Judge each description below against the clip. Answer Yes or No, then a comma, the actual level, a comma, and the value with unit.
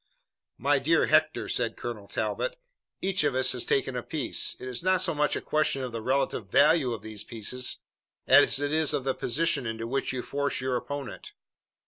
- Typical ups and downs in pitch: Yes, average, 3.1 semitones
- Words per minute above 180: Yes, average, 195 wpm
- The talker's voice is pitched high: No, low, 135 Hz